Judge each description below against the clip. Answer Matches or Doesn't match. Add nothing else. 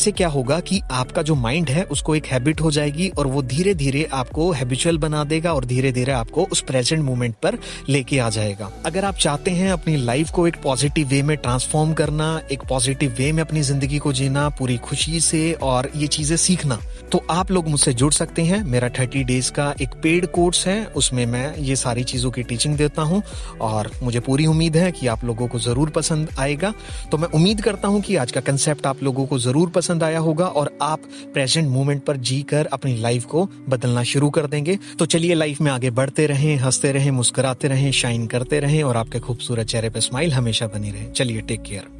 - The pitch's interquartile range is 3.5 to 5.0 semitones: Matches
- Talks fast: Matches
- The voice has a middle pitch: Matches